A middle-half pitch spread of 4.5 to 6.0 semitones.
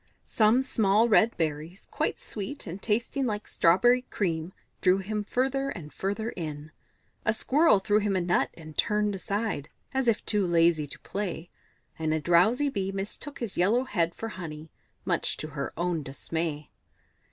Yes: average, 5.0 semitones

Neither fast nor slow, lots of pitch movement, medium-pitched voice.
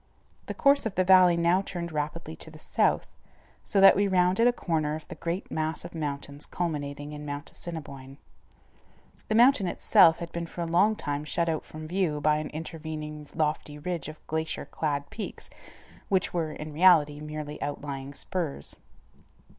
No: average, 170 wpm; average, 3.1 semitones; medium, 160 Hz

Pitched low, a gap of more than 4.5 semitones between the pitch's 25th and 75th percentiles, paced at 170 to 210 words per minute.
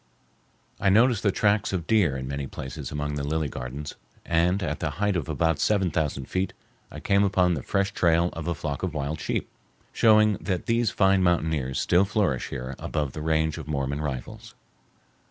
Yes: very low, 80 Hz; average, 5.0 semitones; average, 190 wpm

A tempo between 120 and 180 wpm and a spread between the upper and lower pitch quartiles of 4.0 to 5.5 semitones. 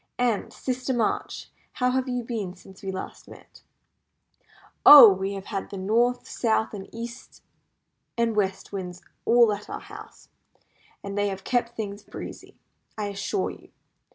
No: average, 150 wpm; average, 3.5 semitones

